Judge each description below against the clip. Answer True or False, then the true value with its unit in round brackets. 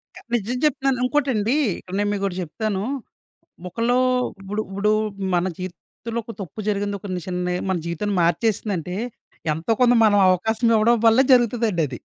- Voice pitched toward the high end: True (205 Hz)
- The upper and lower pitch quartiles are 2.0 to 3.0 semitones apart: False (4.0 semitones)